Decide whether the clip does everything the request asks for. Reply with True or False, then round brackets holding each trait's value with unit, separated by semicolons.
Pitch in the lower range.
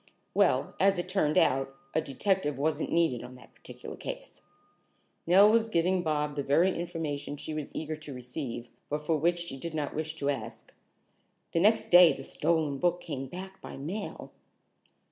False (155 Hz)